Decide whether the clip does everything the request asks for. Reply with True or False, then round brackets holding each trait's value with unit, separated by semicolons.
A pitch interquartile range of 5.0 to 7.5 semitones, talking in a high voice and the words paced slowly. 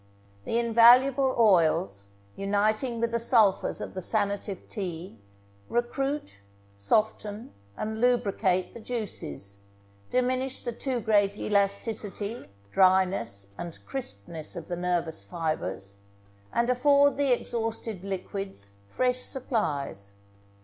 True (5.5 semitones; 205 Hz; 105 wpm)